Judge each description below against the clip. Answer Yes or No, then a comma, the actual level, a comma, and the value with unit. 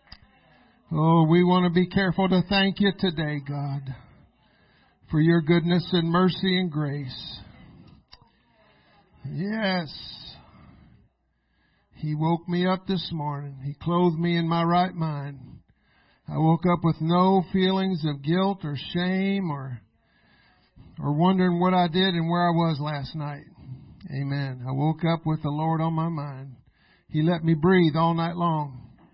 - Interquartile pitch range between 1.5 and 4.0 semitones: Yes, average, 3.7 semitones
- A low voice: No, medium, 165 Hz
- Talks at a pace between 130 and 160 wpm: Yes, average, 145 wpm